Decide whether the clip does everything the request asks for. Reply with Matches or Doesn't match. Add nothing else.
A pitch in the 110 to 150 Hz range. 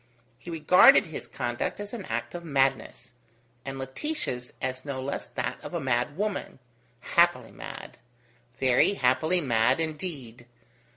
Matches